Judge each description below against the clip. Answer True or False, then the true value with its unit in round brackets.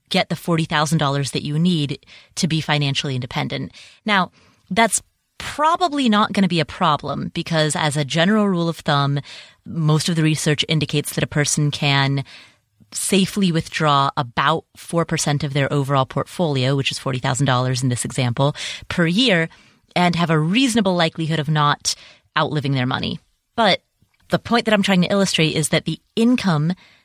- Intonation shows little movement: False (3.8 semitones)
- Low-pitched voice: False (155 Hz)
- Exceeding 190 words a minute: False (160 wpm)